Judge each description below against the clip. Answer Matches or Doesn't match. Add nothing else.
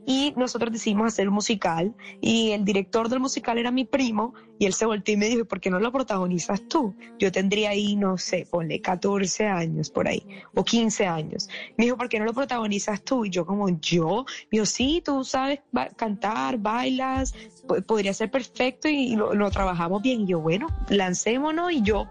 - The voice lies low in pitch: Doesn't match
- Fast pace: Matches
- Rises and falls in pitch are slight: Doesn't match